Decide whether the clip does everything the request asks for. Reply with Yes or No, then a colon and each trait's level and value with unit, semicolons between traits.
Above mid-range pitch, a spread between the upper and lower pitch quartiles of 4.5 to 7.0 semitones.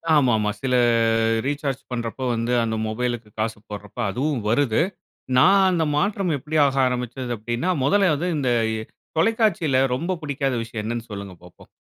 No: low, 130 Hz; average, 4.8 semitones